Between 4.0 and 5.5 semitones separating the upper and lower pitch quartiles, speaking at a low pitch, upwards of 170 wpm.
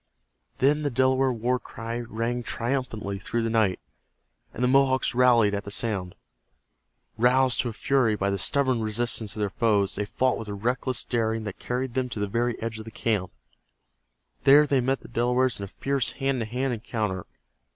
No: average, 3.1 semitones; low, 120 Hz; average, 190 wpm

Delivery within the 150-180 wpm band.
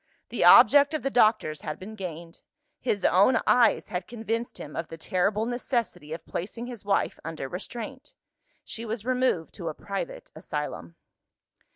Yes: average, 160 wpm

